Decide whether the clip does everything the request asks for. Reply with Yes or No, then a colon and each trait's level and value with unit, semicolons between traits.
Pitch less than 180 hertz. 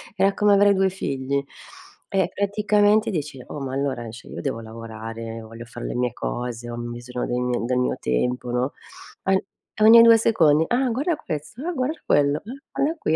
Yes: medium, 140 Hz